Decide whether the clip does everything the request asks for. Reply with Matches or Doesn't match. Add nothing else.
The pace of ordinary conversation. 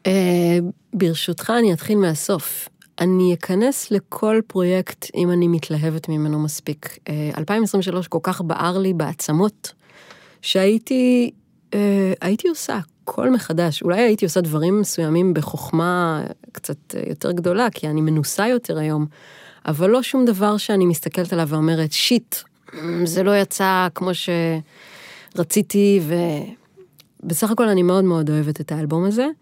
Matches